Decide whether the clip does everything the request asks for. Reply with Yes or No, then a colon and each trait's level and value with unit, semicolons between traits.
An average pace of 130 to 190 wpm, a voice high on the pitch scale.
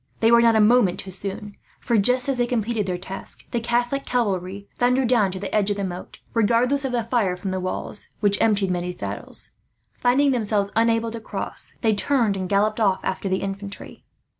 No: fast, 205 wpm; high, 215 Hz